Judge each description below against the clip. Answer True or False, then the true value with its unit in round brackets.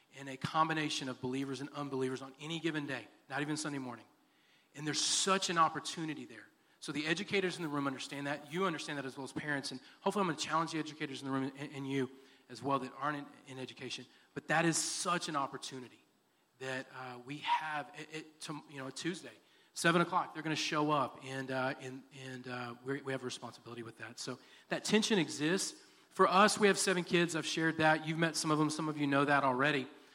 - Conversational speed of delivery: False (230 wpm)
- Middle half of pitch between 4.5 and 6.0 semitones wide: False (3.2 semitones)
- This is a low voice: False (145 Hz)